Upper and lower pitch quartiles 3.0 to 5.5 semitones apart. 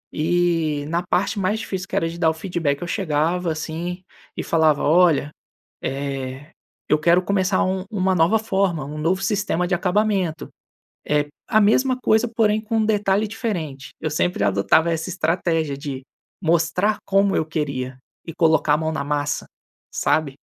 Yes: average, 4.0 semitones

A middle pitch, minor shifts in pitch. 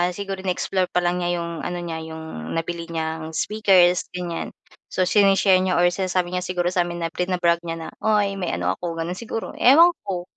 Yes: medium, 175 Hz; narrow, 2.0 semitones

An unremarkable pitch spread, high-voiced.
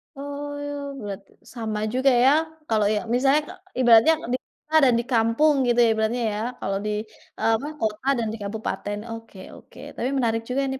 Yes: average, 4.0 semitones; high, 235 Hz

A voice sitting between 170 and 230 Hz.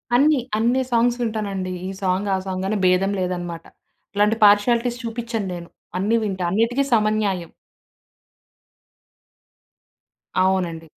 Yes: high, 205 Hz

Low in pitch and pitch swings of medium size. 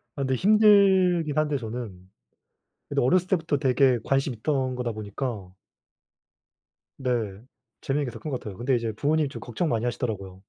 Yes: low, 130 Hz; average, 4.9 semitones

